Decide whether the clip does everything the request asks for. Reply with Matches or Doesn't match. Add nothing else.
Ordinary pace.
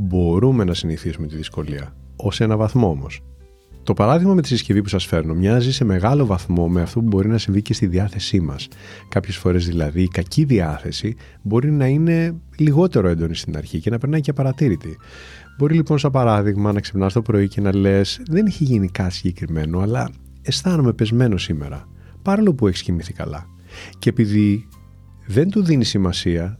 Doesn't match